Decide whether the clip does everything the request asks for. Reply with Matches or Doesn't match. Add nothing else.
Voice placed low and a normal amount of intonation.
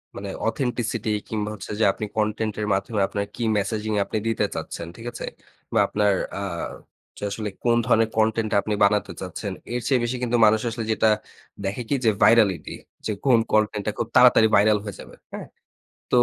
Doesn't match